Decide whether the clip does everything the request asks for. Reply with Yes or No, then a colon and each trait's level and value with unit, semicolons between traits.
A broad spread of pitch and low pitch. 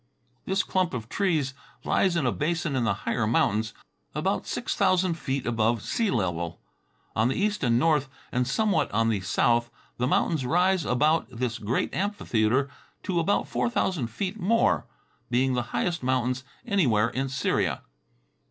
Yes: wide, 6.8 semitones; low, 130 Hz